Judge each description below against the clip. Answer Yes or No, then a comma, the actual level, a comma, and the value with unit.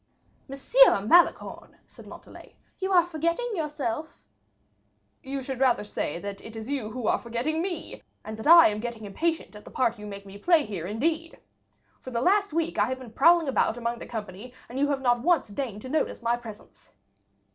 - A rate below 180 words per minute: No, average, 195 wpm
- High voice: Yes, very high, 255 Hz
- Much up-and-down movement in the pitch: Yes, wide, 6.5 semitones